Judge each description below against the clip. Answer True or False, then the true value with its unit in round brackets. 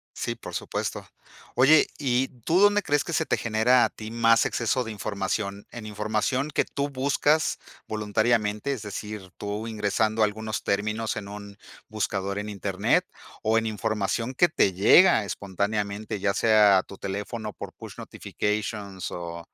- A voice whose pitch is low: True (110 Hz)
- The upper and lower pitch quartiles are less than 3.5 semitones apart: True (2.5 semitones)